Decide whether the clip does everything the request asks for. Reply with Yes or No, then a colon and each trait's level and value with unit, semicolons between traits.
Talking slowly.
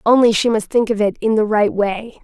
No: fast, 270 wpm